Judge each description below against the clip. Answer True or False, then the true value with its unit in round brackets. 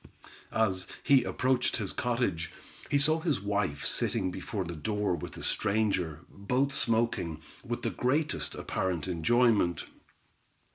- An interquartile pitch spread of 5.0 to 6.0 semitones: True (5.5 semitones)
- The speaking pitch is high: False (105 Hz)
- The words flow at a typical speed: False (130 wpm)